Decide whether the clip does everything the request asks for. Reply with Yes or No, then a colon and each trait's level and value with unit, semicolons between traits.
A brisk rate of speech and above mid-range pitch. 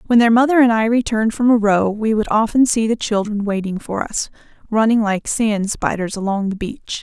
Yes: fast, 215 wpm; high, 215 Hz